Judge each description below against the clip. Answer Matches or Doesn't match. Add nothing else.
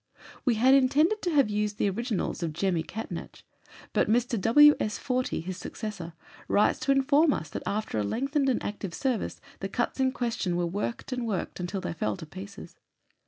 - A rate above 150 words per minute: Matches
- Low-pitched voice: Doesn't match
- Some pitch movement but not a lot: Doesn't match